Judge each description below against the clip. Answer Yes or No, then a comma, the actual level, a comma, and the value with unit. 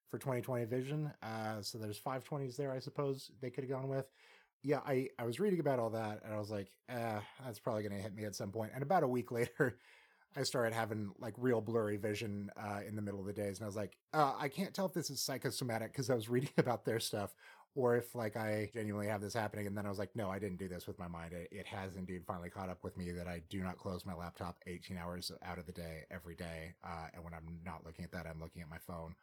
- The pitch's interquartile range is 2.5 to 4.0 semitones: No, average, 5.3 semitones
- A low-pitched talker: Yes, low, 105 Hz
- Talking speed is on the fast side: Yes, fast, 275 wpm